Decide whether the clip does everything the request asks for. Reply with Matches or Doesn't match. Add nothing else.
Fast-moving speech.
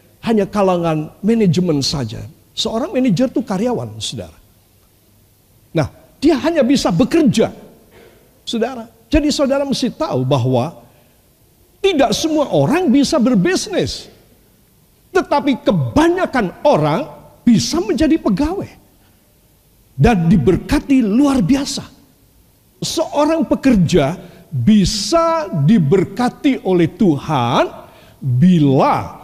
Doesn't match